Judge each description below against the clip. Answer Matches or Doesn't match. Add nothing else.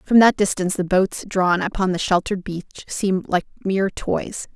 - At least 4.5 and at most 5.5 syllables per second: Matches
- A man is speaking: Doesn't match